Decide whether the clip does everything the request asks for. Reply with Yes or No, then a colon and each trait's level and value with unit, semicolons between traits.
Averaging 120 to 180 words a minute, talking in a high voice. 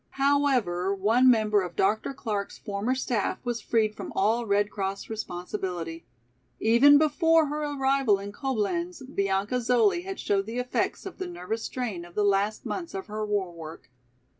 Yes: average, 165 wpm; high, 220 Hz